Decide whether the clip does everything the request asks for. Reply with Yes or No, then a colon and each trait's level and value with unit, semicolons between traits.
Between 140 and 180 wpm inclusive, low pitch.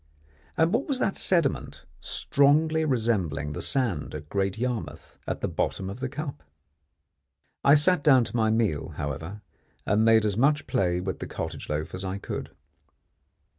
Yes: average, 165 wpm; low, 110 Hz